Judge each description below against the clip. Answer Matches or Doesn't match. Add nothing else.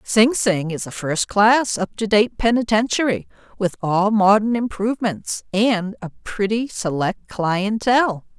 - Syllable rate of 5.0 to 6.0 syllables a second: Doesn't match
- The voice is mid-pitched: Doesn't match